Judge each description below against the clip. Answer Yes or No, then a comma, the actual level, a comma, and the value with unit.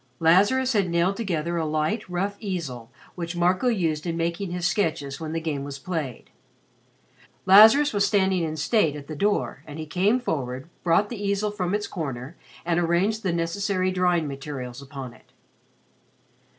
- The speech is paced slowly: No, average, 165 wpm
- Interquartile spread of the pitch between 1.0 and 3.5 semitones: No, average, 4.5 semitones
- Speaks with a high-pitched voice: No, medium, 175 Hz